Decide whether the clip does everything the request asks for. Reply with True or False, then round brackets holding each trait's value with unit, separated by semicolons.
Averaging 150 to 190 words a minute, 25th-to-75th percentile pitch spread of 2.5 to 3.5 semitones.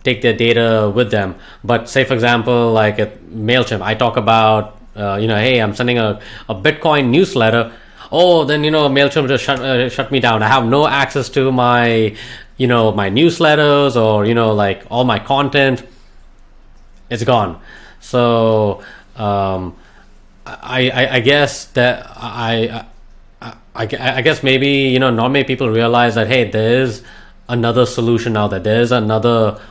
True (170 wpm; 3.2 semitones)